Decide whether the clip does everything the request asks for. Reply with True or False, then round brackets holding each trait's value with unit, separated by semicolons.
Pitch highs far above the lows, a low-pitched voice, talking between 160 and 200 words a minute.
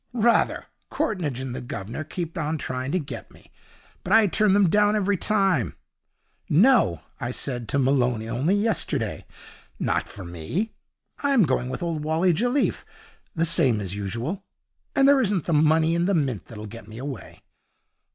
False (8.3 semitones; 155 Hz; 165 wpm)